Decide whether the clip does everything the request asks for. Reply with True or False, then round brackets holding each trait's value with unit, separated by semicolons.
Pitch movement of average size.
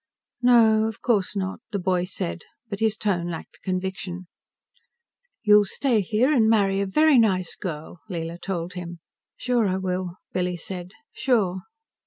True (3.4 semitones)